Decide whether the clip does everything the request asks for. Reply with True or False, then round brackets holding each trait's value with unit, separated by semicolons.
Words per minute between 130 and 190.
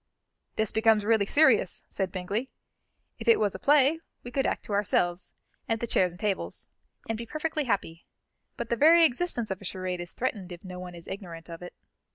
False (205 wpm)